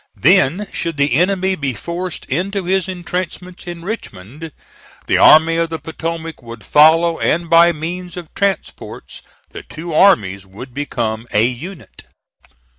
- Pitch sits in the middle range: Yes, medium, 165 Hz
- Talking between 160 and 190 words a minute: No, average, 140 wpm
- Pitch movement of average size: Yes, average, 4.7 semitones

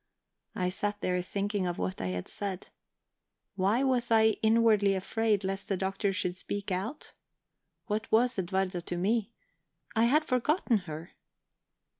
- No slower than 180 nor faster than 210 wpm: No, average, 145 wpm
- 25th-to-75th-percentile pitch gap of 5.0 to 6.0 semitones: No, average, 3.2 semitones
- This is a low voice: No, high, 200 Hz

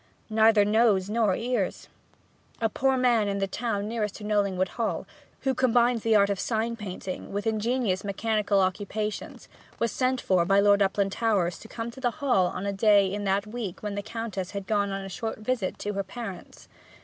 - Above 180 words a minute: Yes, average, 190 wpm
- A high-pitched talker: Yes, high, 210 Hz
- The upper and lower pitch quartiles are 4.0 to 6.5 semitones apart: No, narrow, 2.6 semitones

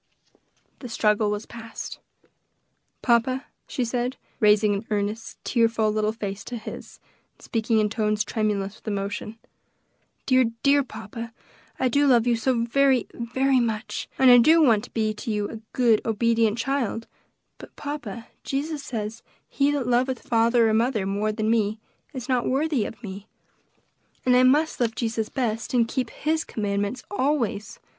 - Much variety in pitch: No, average, 3.1 semitones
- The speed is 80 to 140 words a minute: No, average, 160 wpm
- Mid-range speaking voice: No, high, 230 Hz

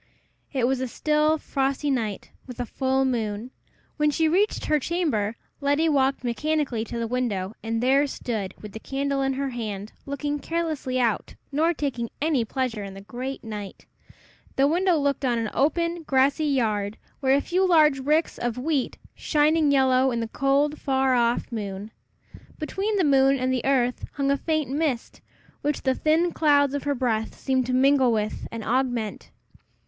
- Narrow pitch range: No, average, 3.8 semitones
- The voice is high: Yes, very high, 270 Hz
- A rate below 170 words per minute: No, average, 175 wpm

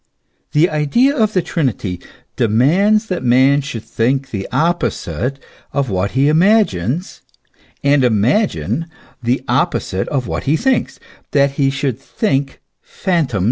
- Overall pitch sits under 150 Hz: Yes, medium, 140 Hz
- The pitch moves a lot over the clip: Yes, wide, 5.7 semitones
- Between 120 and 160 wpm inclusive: Yes, slow, 135 wpm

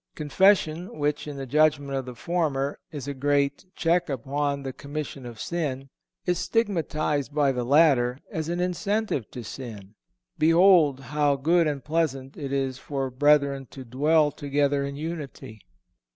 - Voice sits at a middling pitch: Yes, medium, 145 Hz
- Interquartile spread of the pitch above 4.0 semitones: No, average, 2.8 semitones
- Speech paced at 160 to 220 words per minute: No, average, 150 wpm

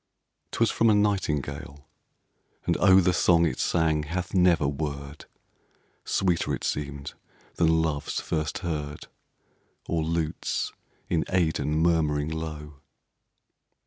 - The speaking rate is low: Yes, slow, 110 wpm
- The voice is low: Yes, very low, 80 Hz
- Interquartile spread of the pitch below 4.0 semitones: Yes, average, 2.8 semitones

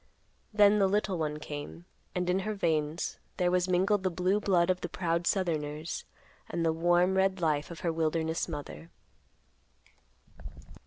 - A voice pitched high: No, medium, 175 Hz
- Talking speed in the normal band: Yes, average, 155 wpm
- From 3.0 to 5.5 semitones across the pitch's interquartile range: No, narrow, 2.6 semitones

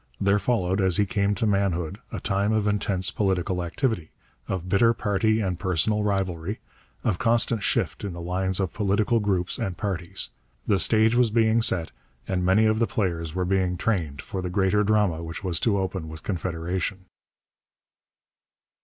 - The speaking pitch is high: No, very low, 95 Hz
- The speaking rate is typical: Yes, average, 170 wpm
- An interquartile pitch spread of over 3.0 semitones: No, average, 2.7 semitones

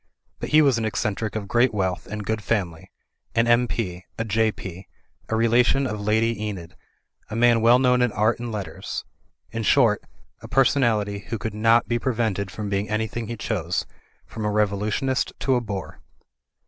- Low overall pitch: Yes, low, 110 Hz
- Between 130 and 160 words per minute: No, average, 185 wpm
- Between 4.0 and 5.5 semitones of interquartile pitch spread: No, narrow, 2.5 semitones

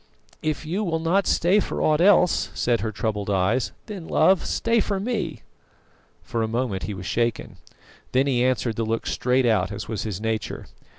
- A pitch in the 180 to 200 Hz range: No, low, 125 Hz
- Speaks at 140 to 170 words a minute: No, average, 185 wpm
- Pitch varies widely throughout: Yes, wide, 7.5 semitones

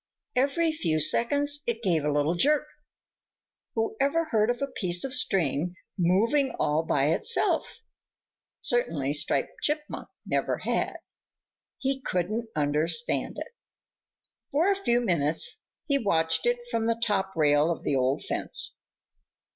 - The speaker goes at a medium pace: No, slow, 130 wpm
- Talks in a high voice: Yes, high, 215 Hz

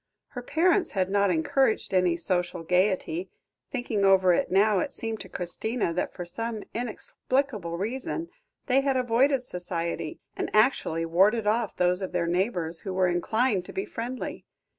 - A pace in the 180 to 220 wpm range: No, average, 160 wpm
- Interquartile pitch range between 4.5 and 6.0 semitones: Yes, wide, 5.4 semitones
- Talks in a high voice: Yes, high, 200 Hz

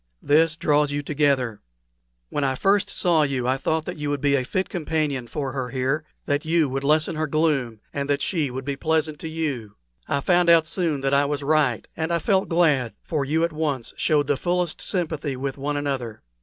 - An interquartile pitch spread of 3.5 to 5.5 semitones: No, average, 2.8 semitones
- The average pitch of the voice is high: No, medium, 145 Hz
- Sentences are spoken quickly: Yes, fast, 210 wpm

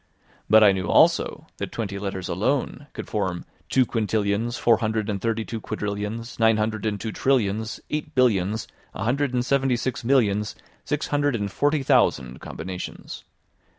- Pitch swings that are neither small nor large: Yes, average, 3.6 semitones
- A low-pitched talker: Yes, low, 110 Hz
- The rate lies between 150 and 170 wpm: Yes, average, 160 wpm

